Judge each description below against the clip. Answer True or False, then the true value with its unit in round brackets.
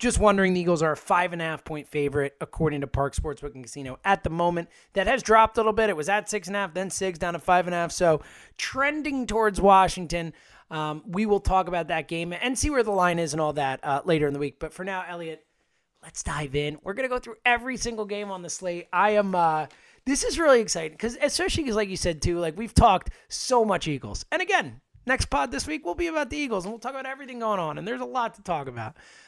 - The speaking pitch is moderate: True (180 Hz)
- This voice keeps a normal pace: False (265 wpm)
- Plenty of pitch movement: True (5.9 semitones)